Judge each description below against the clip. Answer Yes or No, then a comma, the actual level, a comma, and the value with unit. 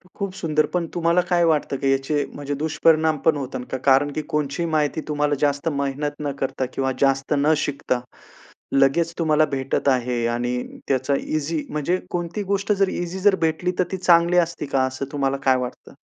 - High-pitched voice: No, medium, 150 Hz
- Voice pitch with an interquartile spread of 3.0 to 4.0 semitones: Yes, average, 3.6 semitones